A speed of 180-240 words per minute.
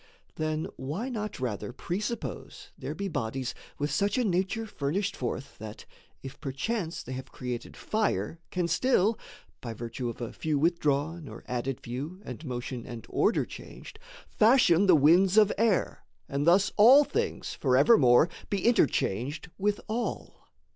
No: average, 145 wpm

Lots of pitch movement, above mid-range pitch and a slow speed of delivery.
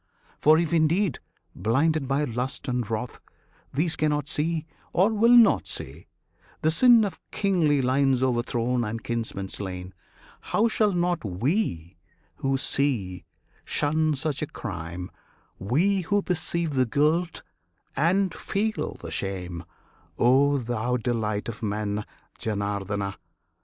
No: wide, 7.4 semitones; low, 135 Hz; slow, 125 wpm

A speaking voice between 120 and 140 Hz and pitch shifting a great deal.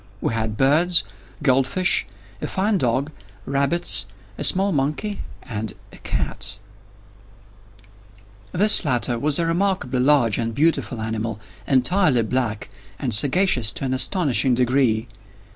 Yes: low, 135 Hz; wide, 6.3 semitones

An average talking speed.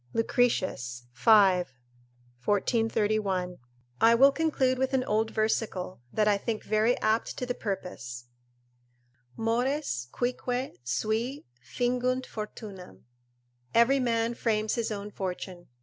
No: slow, 110 wpm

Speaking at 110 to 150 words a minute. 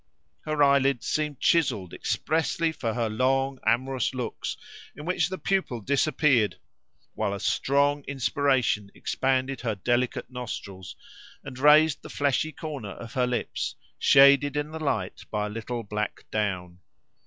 Yes: average, 140 wpm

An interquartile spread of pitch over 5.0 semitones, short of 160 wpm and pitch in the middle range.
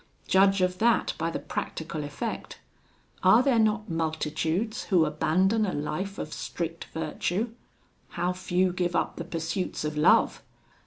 No: average, 3.5 semitones; average, 145 wpm; medium, 180 Hz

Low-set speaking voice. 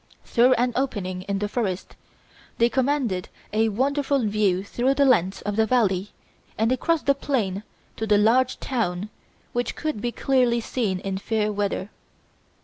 No: high, 225 Hz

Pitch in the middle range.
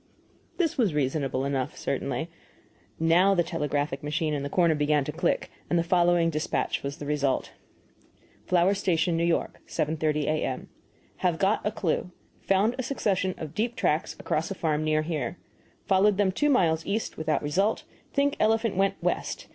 Yes: medium, 165 Hz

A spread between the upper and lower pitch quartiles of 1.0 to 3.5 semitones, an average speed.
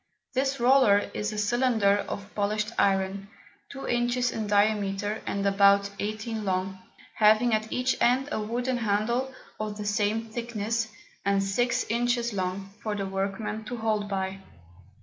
Yes: average, 3.0 semitones; average, 150 wpm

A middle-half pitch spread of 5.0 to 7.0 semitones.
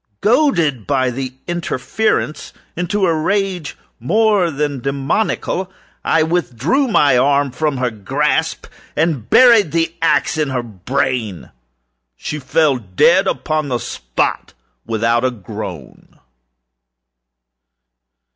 Yes: wide, 5.4 semitones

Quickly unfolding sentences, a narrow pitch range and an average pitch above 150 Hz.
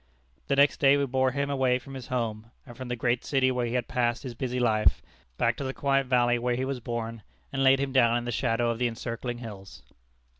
No: fast, 240 wpm; narrow, 2.1 semitones; low, 125 Hz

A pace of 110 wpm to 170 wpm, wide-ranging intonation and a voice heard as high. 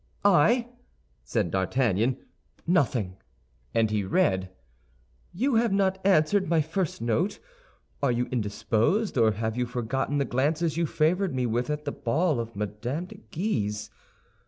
No: average, 140 wpm; wide, 7.6 semitones; low, 135 Hz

